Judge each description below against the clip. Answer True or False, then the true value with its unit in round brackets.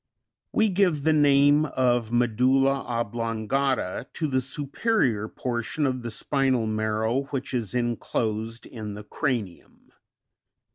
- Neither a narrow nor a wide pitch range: True (3.8 semitones)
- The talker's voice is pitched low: True (125 Hz)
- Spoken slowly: True (125 wpm)